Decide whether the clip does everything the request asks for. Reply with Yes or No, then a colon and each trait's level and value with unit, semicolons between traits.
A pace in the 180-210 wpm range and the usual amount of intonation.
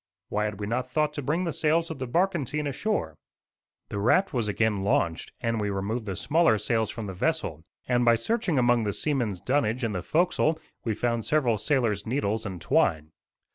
No: average, 195 wpm; wide, 6.3 semitones